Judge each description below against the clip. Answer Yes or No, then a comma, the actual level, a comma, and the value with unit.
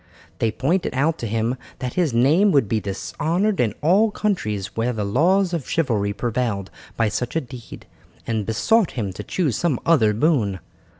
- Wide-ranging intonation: Yes, wide, 7.3 semitones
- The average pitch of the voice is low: Yes, low, 125 Hz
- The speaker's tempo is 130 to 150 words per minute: No, average, 175 wpm